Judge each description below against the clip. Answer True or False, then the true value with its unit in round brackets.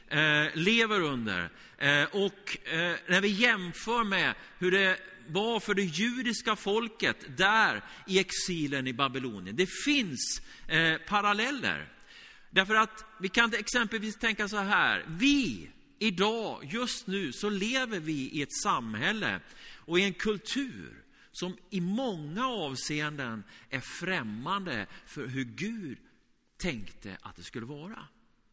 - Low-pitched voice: False (200 Hz)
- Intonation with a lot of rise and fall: True (6.1 semitones)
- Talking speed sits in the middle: False (120 wpm)